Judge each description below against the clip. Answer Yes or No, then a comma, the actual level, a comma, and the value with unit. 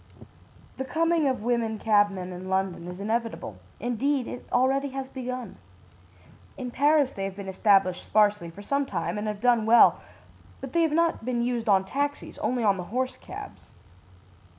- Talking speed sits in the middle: Yes, average, 170 wpm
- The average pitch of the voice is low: No, high, 235 Hz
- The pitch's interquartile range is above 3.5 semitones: Yes, average, 4.8 semitones